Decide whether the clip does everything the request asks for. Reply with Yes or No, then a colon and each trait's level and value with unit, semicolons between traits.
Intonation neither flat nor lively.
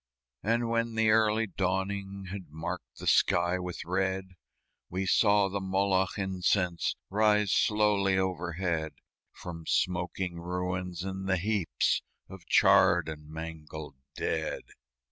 No: narrow, 2.3 semitones